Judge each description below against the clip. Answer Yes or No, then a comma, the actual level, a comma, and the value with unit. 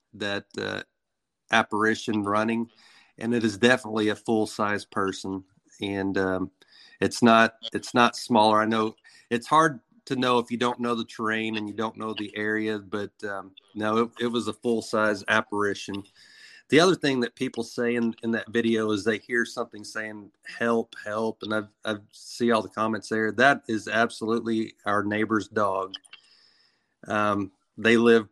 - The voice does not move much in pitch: Yes, narrow, 1.8 semitones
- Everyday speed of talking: Yes, average, 170 wpm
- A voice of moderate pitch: No, low, 110 Hz